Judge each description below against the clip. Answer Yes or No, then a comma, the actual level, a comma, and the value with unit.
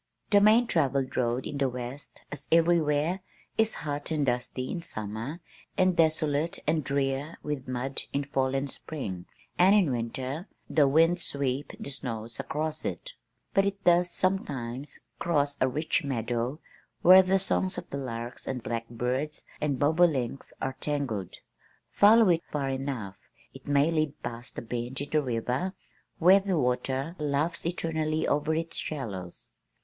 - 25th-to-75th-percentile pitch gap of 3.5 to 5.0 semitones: Yes, average, 4.4 semitones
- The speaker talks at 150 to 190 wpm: Yes, average, 155 wpm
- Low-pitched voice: No, medium, 145 Hz